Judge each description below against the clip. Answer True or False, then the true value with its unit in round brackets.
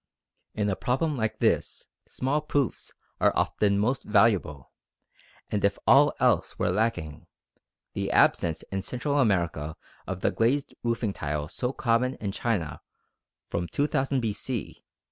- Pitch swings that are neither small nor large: False (5.7 semitones)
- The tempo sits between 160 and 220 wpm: False (140 wpm)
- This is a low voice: True (110 Hz)